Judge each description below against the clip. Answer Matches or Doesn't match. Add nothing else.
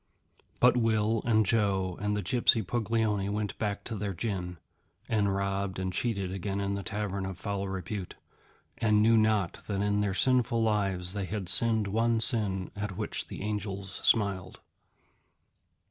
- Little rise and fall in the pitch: Matches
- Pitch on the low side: Matches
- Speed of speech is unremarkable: Matches